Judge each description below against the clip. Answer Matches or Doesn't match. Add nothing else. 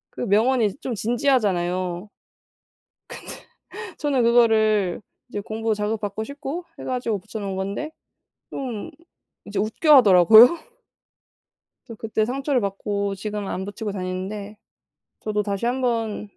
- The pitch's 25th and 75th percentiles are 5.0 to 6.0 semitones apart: Doesn't match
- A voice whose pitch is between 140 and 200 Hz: Doesn't match